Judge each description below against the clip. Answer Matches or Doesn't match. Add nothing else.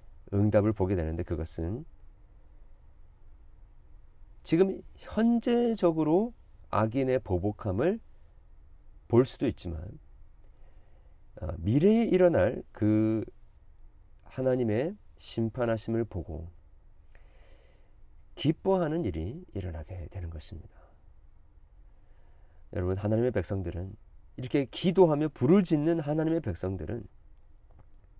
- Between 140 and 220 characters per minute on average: Matches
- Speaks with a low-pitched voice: Matches